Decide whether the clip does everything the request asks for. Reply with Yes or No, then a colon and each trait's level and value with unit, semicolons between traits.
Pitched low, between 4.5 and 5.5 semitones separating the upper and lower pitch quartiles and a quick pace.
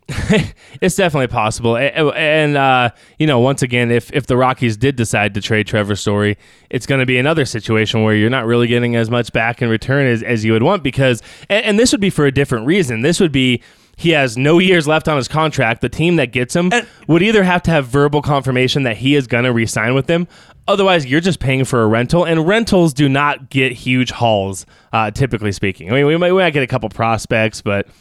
Yes: low, 130 Hz; average, 5.0 semitones; fast, 235 wpm